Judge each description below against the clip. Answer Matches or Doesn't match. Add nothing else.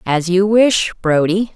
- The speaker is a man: Doesn't match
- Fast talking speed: Doesn't match